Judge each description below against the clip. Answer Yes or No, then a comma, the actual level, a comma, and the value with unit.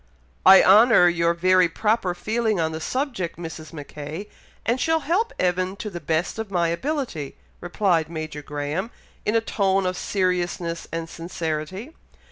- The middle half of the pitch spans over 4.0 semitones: Yes, average, 4.4 semitones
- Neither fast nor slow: Yes, average, 150 wpm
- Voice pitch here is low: No, medium, 180 Hz